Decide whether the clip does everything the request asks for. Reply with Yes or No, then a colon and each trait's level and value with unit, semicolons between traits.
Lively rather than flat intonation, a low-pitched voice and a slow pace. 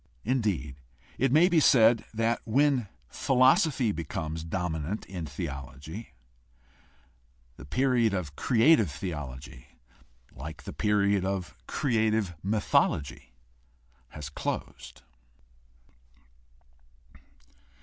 Yes: wide, 7.5 semitones; low, 100 Hz; slow, 85 wpm